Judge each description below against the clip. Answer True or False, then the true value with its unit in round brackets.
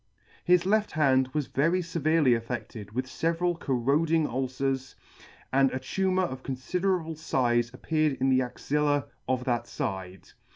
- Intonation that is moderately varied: True (4.3 semitones)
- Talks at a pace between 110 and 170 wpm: True (150 wpm)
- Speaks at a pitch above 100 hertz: True (135 Hz)